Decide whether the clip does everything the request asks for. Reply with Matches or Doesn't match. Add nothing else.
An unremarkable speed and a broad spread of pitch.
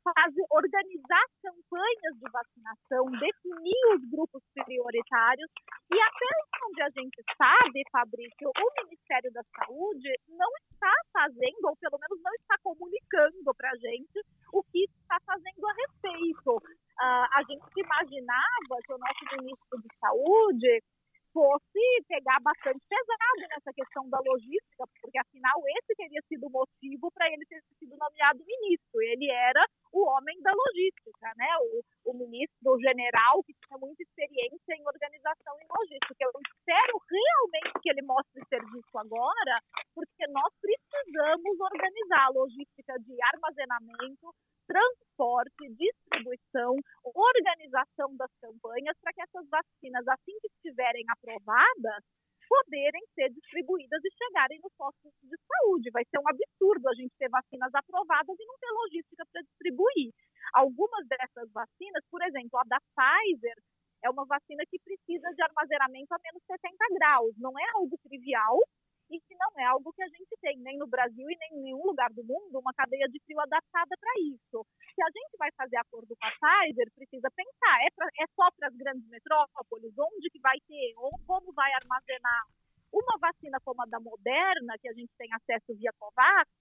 Matches